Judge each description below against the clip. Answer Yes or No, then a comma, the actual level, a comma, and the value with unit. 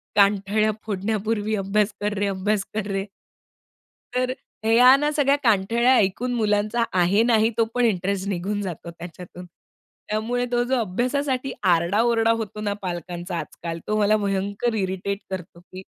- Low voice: No, high, 210 Hz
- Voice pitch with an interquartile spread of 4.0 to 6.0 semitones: No, average, 3.1 semitones